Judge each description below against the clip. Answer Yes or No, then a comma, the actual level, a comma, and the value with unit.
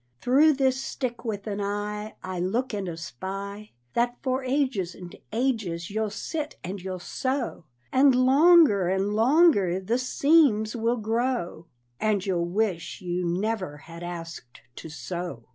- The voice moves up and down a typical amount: No, wide, 6.0 semitones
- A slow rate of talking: No, average, 145 wpm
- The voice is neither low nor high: No, high, 210 Hz